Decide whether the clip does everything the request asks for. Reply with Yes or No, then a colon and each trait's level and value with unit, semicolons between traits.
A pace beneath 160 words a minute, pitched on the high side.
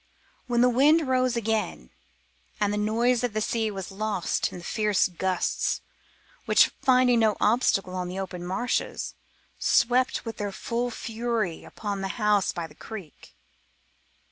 Yes: average, 150 wpm; high, 215 Hz